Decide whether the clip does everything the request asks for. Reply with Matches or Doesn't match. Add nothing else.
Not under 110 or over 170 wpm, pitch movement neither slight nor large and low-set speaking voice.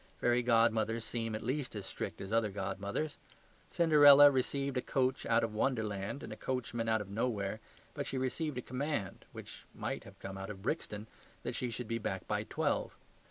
Doesn't match